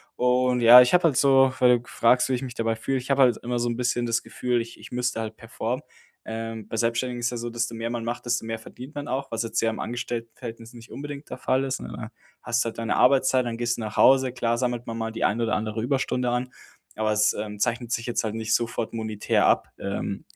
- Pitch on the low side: Yes, low, 120 Hz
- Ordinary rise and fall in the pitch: No, narrow, 1.7 semitones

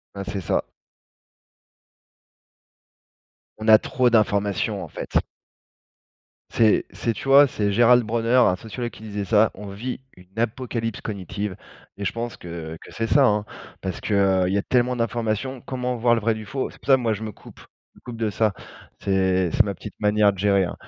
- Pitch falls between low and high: No, low, 110 Hz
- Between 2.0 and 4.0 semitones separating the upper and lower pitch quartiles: Yes, average, 2.9 semitones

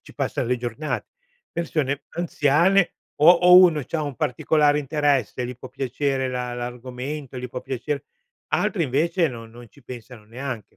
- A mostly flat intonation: No, average, 3.6 semitones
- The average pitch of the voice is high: No, low, 135 Hz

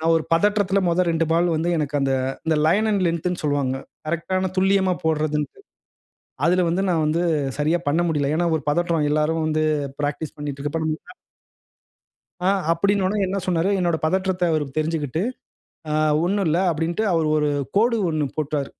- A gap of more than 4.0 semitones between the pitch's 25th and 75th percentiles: No, average, 3.1 semitones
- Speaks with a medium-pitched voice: Yes, medium, 165 Hz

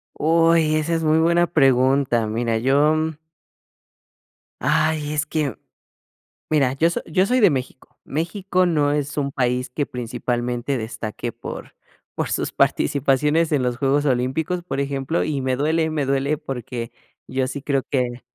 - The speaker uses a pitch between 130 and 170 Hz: Yes, medium, 140 Hz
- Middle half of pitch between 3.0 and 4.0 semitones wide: Yes, average, 3.6 semitones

